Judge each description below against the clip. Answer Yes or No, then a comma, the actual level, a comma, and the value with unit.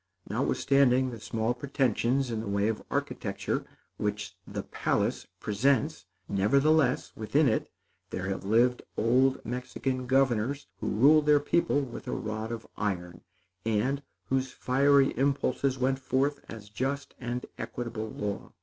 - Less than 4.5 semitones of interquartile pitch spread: Yes, average, 3.9 semitones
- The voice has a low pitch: Yes, low, 125 Hz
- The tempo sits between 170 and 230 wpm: No, slow, 135 wpm